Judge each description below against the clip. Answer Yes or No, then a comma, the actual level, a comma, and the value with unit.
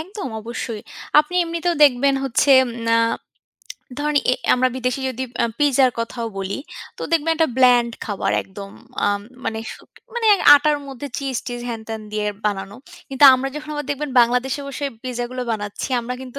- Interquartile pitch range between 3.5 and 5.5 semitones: Yes, average, 4.0 semitones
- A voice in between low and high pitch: No, very high, 255 Hz